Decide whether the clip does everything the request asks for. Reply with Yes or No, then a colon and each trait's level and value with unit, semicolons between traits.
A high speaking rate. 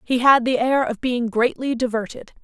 No: average, 195 wpm